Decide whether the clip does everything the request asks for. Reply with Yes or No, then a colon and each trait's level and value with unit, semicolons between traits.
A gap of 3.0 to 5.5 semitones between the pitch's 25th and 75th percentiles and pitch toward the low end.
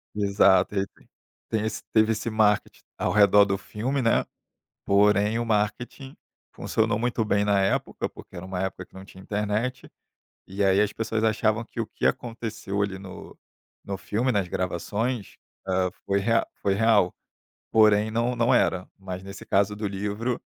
No: narrow, 2.4 semitones; low, 105 Hz